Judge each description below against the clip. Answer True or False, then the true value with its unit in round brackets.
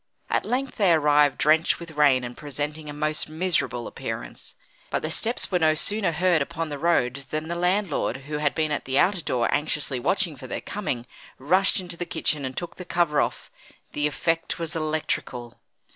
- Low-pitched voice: False (155 Hz)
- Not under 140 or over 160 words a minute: False (190 wpm)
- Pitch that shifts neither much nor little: True (3.0 semitones)